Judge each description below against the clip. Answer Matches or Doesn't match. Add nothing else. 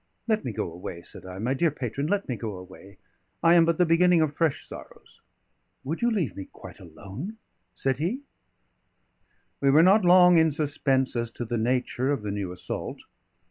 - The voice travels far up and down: Matches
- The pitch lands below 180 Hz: Matches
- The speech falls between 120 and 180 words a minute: Doesn't match